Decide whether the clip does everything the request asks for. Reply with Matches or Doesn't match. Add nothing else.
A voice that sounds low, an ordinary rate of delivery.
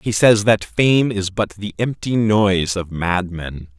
Matches